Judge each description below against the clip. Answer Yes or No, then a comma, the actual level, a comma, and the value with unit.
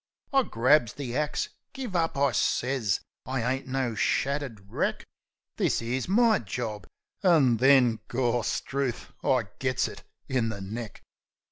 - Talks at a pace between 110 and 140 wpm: Yes, slow, 135 wpm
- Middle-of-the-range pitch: No, low, 130 Hz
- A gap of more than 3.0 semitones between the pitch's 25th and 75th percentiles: Yes, average, 3.4 semitones